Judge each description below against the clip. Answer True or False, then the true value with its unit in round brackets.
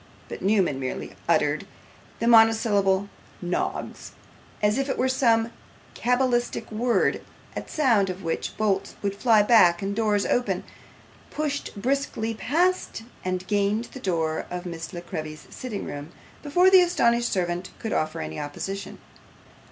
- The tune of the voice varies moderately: True (4.9 semitones)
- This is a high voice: True (210 Hz)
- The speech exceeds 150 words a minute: False (140 wpm)